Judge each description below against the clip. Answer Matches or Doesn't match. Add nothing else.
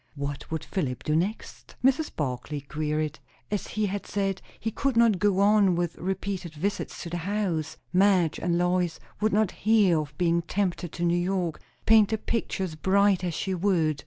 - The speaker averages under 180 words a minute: Doesn't match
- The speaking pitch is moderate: Matches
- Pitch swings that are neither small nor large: Matches